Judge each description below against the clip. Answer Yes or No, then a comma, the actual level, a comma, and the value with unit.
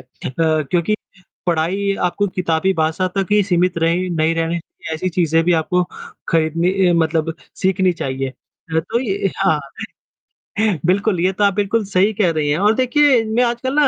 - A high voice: No, medium, 180 Hz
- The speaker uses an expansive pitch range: No, average, 3.7 semitones